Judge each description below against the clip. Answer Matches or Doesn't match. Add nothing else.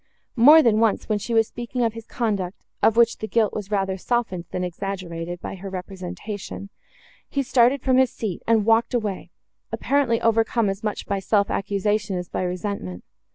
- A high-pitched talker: Matches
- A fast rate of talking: Doesn't match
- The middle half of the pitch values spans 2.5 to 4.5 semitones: Matches